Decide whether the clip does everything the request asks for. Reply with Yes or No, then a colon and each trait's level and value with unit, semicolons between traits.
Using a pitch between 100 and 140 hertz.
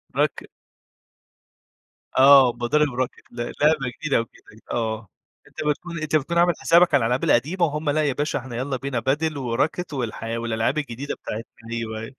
Yes: low, 135 Hz